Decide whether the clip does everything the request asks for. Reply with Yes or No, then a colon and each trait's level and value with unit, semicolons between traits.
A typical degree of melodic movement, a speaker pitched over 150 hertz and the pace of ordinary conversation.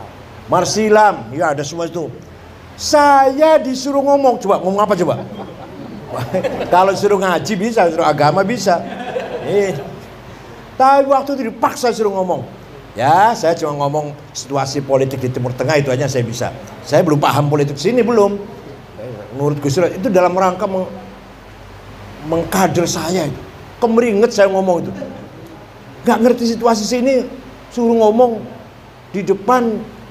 No: wide, 8.2 semitones; medium, 185 Hz; average, 130 wpm